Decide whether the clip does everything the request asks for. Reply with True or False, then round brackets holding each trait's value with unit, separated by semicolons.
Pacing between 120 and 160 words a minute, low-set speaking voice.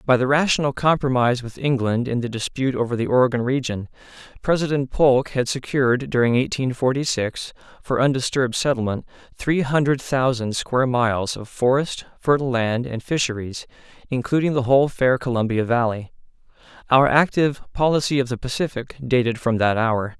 True (150 wpm; 130 Hz)